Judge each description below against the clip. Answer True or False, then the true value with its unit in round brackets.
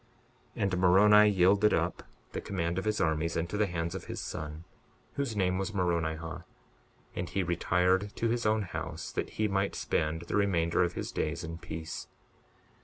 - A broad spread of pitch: False (3.5 semitones)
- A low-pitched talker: True (90 Hz)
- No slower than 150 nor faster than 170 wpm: False (180 wpm)